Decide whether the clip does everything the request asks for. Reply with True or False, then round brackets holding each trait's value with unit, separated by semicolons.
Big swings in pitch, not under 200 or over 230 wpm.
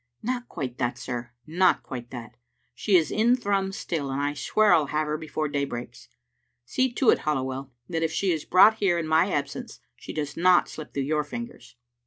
True (6.0 semitones; 205 wpm)